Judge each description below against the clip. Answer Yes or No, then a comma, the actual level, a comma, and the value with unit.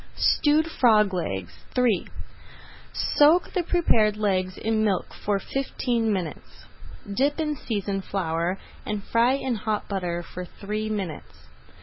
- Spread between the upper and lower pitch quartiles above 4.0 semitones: Yes, average, 5.0 semitones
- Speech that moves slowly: Yes, slow, 125 wpm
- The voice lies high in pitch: Yes, high, 210 Hz